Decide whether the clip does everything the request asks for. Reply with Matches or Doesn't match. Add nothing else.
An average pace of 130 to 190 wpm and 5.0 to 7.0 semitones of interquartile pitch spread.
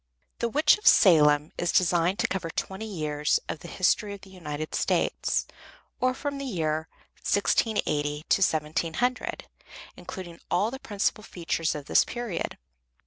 Matches